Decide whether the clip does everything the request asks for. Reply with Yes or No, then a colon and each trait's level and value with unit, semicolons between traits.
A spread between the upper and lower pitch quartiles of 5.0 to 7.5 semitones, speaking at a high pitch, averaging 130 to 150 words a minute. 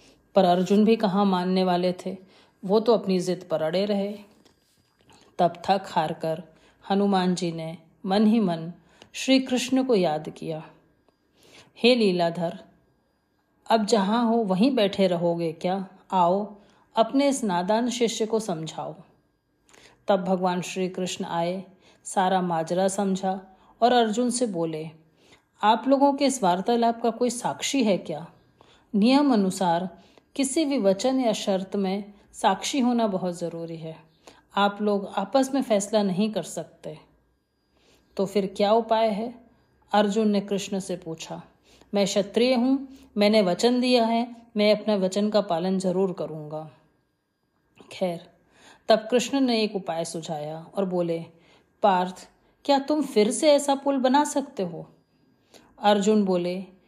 No: average, 4.3 semitones; high, 200 Hz; average, 140 wpm